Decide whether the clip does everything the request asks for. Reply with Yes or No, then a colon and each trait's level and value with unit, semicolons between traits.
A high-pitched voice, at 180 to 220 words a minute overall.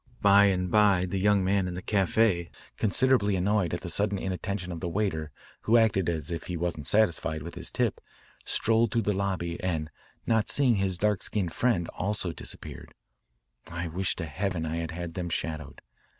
No: very low, 95 Hz; average, 185 wpm